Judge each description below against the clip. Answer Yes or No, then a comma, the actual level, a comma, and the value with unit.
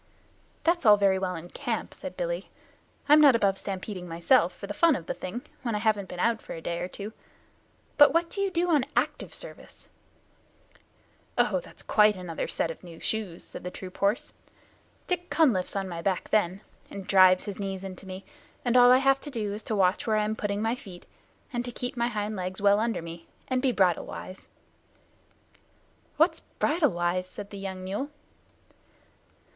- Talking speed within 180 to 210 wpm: Yes, average, 195 wpm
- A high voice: Yes, high, 205 Hz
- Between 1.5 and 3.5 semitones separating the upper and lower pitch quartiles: No, average, 4.8 semitones